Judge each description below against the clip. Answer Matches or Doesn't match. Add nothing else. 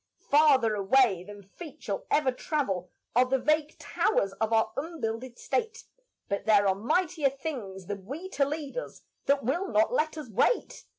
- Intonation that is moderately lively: Doesn't match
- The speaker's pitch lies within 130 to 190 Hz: Doesn't match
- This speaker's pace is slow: Doesn't match